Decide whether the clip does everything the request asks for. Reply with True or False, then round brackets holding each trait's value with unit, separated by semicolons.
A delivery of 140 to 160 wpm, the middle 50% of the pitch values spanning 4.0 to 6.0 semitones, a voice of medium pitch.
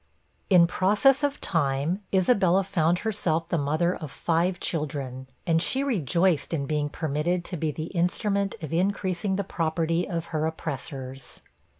False (150 wpm; 3.5 semitones; 170 Hz)